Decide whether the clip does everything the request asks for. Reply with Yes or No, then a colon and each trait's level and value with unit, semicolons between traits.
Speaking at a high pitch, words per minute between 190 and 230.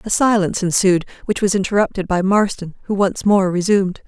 No: high, 195 Hz; average, 175 wpm